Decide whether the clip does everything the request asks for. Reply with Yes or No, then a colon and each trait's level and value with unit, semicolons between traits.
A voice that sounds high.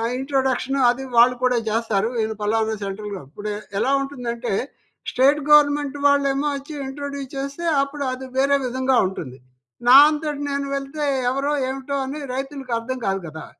Yes: very high, 265 Hz